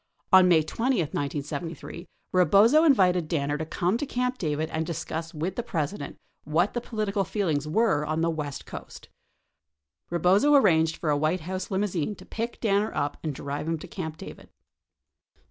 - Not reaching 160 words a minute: No, average, 165 wpm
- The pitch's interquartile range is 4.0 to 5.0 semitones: Yes, average, 4.6 semitones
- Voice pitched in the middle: Yes, medium, 170 Hz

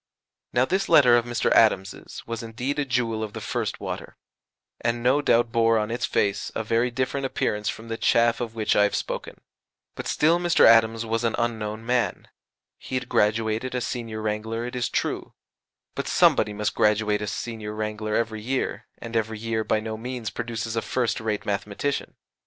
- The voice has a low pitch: Yes, low, 115 Hz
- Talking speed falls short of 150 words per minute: No, average, 185 wpm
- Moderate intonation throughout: No, narrow, 1.9 semitones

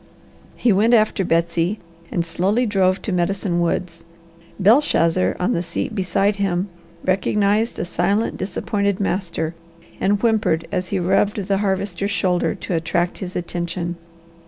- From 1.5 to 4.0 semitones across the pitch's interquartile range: Yes, average, 2.7 semitones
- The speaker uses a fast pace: No, slow, 135 wpm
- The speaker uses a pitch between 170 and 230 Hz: Yes, high, 190 Hz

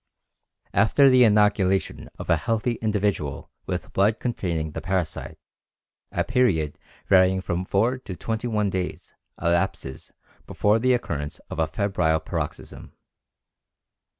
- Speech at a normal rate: No, slow, 125 wpm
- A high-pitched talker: No, very low, 95 Hz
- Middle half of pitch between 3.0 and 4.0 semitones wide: No, average, 4.7 semitones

